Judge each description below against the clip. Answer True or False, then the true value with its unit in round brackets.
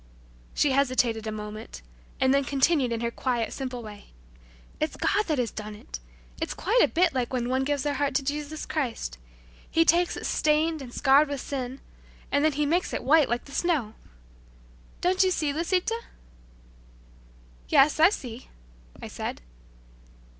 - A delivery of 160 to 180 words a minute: True (170 wpm)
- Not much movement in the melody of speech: False (4.2 semitones)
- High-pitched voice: True (280 Hz)